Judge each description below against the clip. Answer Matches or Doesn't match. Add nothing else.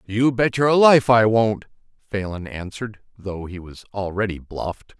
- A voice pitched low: Matches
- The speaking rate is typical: Matches